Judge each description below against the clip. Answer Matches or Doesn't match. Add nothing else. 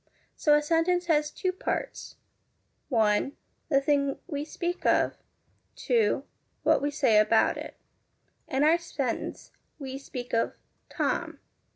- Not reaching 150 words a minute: Matches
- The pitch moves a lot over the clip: Doesn't match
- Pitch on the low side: Doesn't match